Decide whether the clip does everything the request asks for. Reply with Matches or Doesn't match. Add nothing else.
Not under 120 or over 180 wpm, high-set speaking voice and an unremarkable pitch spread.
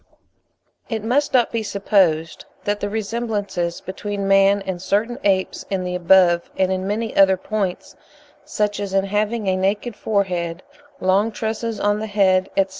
Doesn't match